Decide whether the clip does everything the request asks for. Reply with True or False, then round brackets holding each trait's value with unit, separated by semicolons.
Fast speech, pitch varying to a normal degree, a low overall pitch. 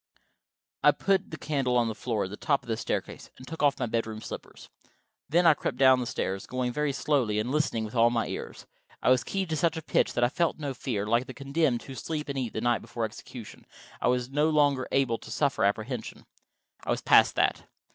True (230 wpm; 4.2 semitones; 130 Hz)